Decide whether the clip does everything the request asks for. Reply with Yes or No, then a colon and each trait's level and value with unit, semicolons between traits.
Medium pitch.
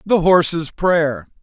Yes: medium, 170 Hz